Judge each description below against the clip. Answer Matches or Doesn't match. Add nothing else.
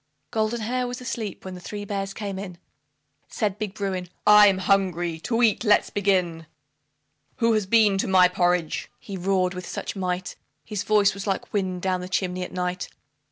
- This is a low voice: Doesn't match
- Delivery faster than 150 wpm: Matches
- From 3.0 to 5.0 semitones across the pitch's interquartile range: Doesn't match